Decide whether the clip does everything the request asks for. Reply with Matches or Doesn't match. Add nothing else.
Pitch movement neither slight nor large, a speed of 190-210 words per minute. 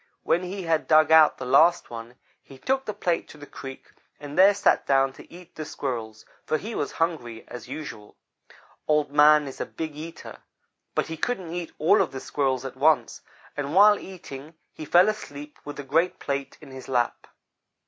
Matches